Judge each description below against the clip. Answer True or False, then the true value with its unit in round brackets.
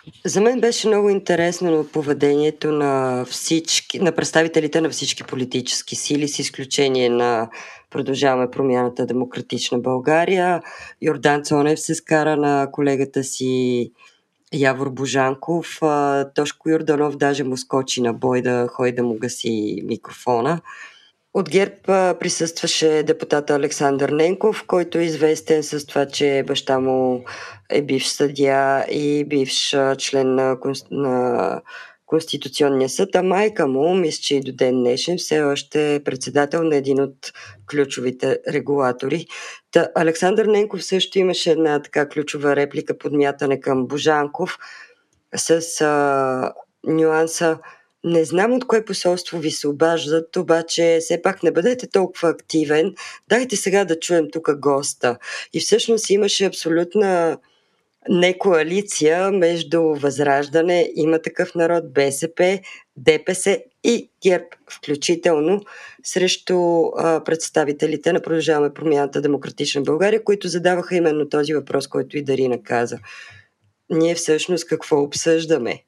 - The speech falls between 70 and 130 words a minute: True (125 wpm)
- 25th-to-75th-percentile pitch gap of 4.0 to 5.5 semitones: False (3.6 semitones)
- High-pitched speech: False (155 Hz)